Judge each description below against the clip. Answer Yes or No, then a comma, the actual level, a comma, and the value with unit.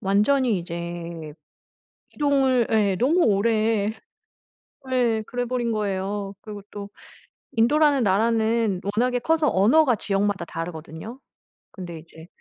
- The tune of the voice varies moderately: Yes, average, 4.5 semitones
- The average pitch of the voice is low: No, high, 215 Hz